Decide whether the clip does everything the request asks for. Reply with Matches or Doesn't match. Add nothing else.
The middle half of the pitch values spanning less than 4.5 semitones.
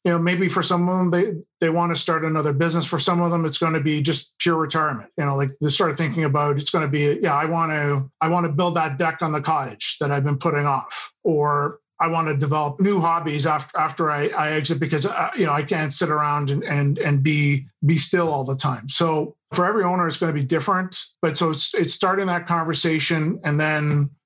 Matches